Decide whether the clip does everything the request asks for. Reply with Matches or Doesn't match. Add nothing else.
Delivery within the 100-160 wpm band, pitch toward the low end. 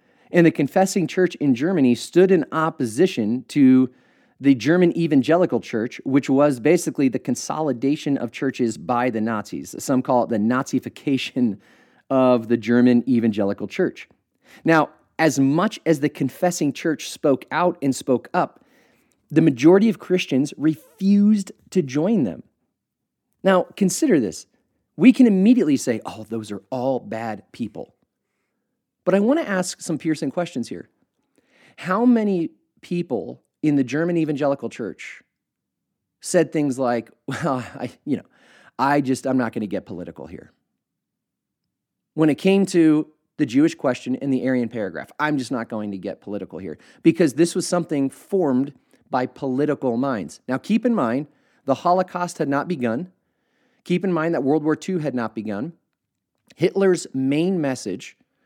Doesn't match